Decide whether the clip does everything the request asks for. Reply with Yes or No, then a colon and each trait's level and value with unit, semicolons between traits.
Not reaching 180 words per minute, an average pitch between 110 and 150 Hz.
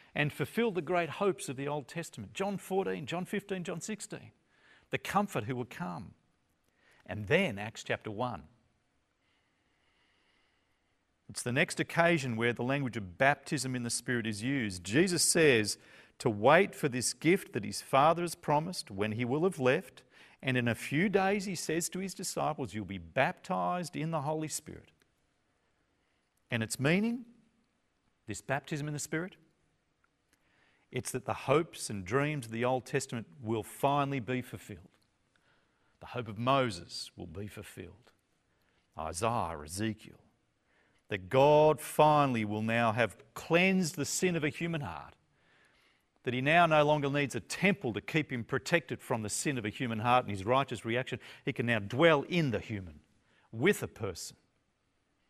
Yes: average, 165 wpm; low, 135 Hz